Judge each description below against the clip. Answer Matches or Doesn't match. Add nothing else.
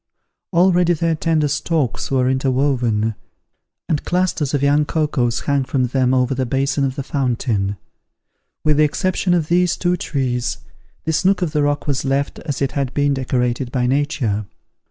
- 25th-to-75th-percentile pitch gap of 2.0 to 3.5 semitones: Matches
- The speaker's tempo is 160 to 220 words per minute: Matches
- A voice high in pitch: Doesn't match